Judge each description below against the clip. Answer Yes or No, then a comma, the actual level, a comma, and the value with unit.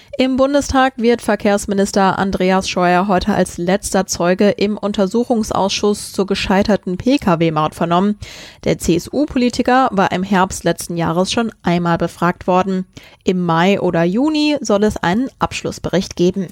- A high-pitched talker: Yes, high, 195 Hz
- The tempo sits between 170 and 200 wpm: No, average, 130 wpm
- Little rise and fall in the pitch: No, average, 3.3 semitones